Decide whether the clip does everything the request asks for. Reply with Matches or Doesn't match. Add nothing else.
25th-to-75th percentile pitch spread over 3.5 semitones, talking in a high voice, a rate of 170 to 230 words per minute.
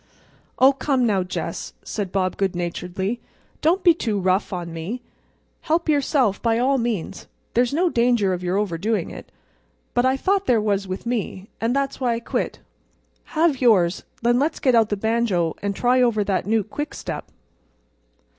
Matches